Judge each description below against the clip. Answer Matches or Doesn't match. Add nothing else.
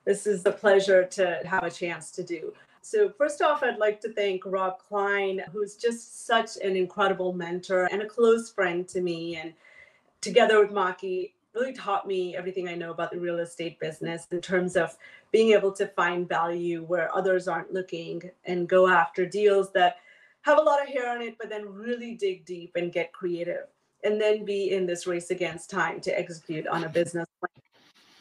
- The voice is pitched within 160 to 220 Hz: Matches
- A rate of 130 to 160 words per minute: Doesn't match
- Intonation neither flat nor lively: Matches